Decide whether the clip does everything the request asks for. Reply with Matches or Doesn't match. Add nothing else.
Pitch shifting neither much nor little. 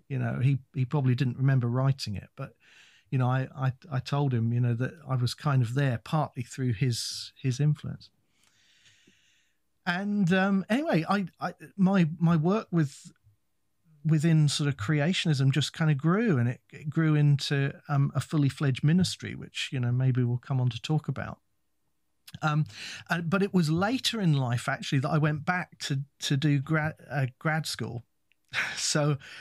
Matches